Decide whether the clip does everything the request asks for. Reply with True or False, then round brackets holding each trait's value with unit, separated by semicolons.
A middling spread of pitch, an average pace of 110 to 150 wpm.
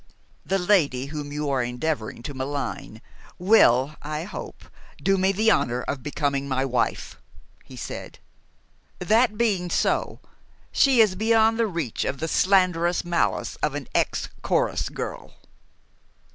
False (6.0 semitones; 140 wpm)